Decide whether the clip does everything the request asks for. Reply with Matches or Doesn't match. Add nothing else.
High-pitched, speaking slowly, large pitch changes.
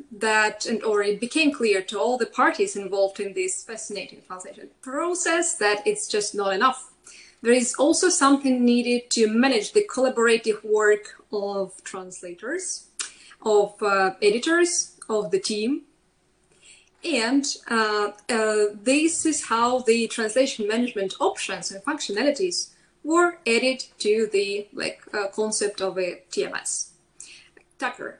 Matches